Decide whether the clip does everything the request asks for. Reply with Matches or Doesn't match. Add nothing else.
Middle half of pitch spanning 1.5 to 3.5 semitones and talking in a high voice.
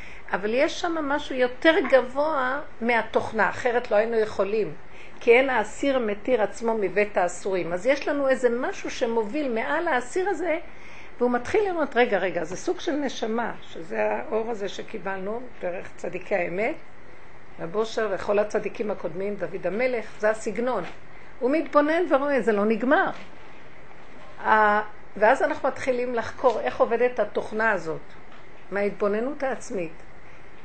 Doesn't match